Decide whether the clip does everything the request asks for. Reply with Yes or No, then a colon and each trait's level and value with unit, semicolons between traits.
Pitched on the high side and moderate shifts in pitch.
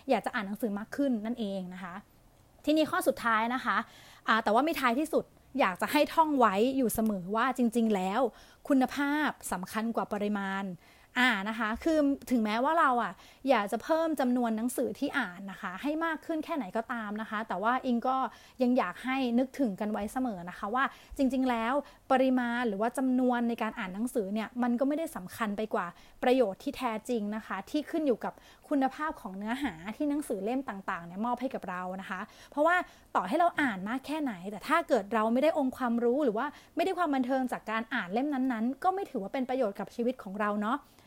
Yes: high, 245 Hz; average, 3.9 semitones